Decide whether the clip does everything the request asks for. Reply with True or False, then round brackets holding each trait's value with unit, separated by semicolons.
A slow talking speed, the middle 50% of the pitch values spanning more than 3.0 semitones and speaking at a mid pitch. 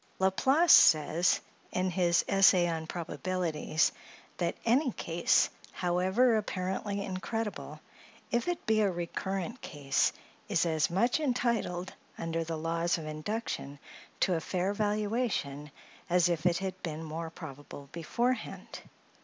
True (130 wpm; 4.2 semitones; 180 Hz)